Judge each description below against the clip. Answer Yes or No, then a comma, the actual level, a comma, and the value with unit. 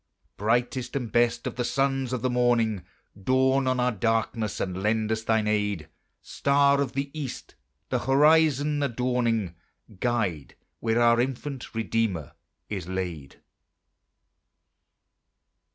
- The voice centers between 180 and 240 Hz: No, low, 120 Hz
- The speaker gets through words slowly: Yes, slow, 120 wpm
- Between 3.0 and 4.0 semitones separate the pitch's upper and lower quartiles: Yes, average, 3.6 semitones